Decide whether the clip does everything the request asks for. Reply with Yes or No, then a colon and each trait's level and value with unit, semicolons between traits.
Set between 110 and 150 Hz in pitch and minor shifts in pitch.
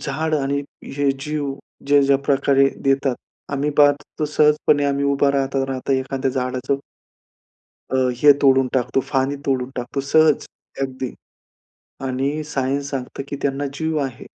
Yes: medium, 140 Hz; narrow, 1.3 semitones